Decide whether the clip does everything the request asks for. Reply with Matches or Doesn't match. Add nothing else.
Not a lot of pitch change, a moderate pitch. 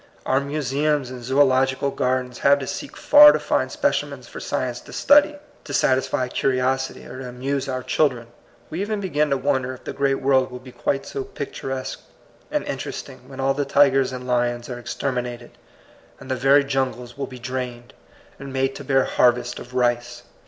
Doesn't match